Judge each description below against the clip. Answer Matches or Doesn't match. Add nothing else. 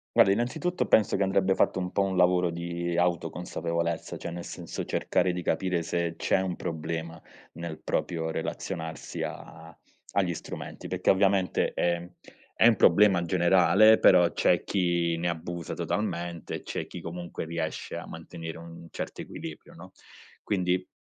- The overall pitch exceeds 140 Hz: Doesn't match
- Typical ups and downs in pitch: Doesn't match